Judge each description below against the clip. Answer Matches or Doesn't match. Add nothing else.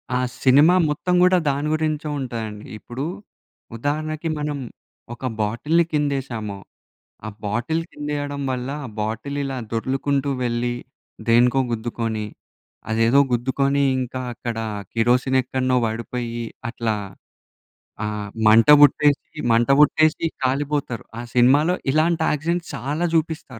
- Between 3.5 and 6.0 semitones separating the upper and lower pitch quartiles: Matches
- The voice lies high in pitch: Doesn't match